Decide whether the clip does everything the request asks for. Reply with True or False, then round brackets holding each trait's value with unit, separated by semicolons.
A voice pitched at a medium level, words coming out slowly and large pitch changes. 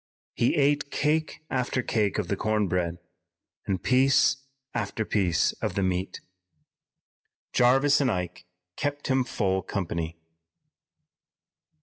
False (110 Hz; 115 wpm; 6.3 semitones)